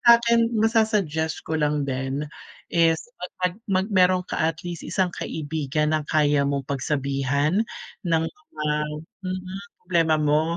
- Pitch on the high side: No, medium, 160 Hz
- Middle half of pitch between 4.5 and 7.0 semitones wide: No, average, 3.9 semitones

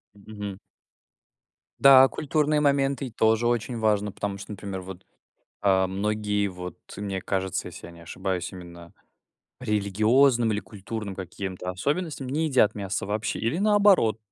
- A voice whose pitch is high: No, low, 105 Hz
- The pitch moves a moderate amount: Yes, average, 4.9 semitones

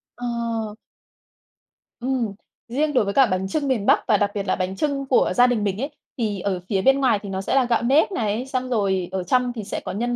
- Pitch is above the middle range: Yes, high, 230 Hz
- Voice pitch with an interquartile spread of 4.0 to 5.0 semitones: Yes, average, 4.3 semitones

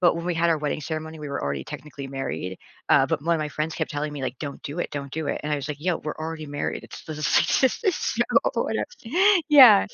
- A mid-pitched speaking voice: Yes, medium, 150 Hz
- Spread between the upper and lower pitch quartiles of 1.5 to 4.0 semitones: Yes, narrow, 2.4 semitones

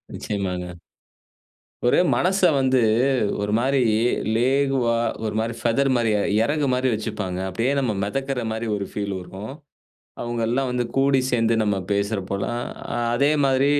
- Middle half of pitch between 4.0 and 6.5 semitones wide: Yes, average, 4.5 semitones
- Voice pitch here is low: Yes, low, 120 Hz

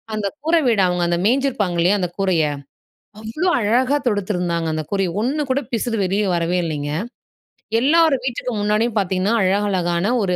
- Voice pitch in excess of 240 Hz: No, high, 205 Hz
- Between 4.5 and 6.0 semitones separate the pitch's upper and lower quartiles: Yes, average, 5.1 semitones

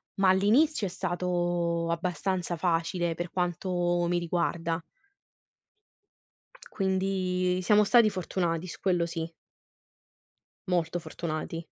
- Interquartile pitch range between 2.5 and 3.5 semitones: No, narrow, 1.8 semitones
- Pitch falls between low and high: Yes, medium, 175 Hz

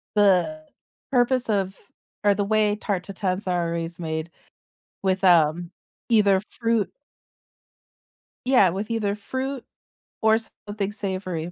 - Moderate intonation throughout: Yes, average, 3.2 semitones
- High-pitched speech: Yes, high, 200 Hz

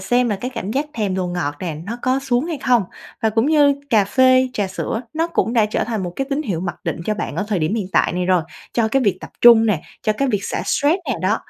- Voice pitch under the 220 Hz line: No, high, 225 Hz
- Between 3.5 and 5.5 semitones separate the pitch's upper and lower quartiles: Yes, average, 5.2 semitones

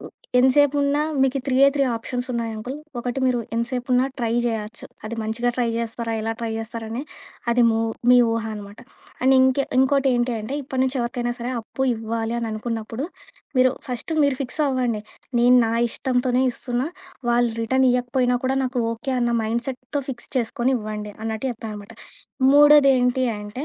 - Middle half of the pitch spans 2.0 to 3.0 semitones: Yes, narrow, 2.4 semitones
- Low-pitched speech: No, high, 245 Hz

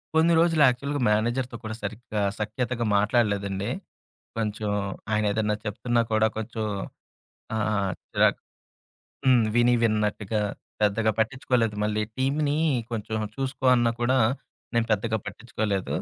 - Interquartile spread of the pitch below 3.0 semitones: Yes, narrow, 2.6 semitones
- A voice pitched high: No, low, 110 Hz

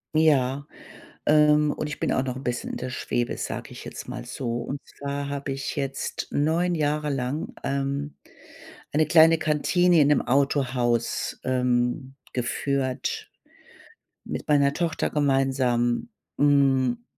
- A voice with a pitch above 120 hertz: Yes, medium, 140 Hz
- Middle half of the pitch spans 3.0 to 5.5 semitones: No, narrow, 2.6 semitones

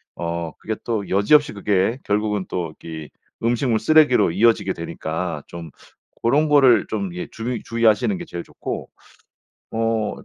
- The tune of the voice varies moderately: Yes, average, 4.9 semitones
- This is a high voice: No, low, 105 Hz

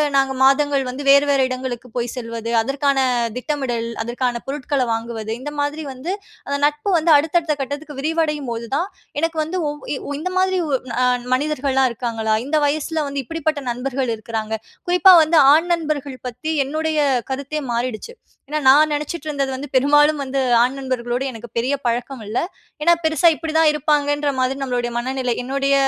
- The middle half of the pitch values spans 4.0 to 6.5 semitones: No, average, 3.3 semitones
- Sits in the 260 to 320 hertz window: Yes, very high, 275 Hz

